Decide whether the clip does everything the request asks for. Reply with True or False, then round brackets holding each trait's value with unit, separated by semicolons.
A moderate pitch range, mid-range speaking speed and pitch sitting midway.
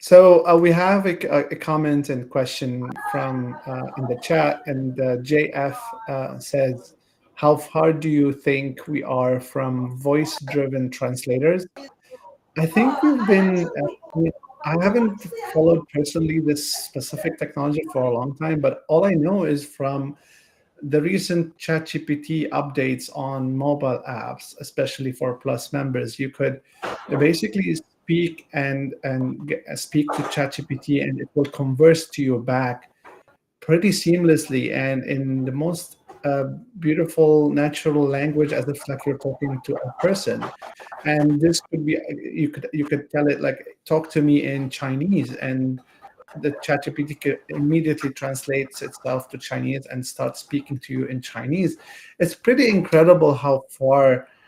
True (3.0 semitones; 145 wpm; 145 Hz)